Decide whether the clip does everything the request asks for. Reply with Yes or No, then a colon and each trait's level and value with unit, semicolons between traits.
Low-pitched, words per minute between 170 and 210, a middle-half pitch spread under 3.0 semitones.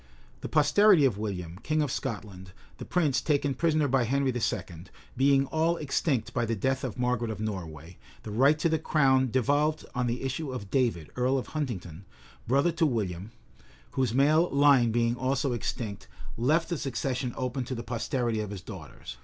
No: low, 130 Hz; average, 180 wpm; average, 4.3 semitones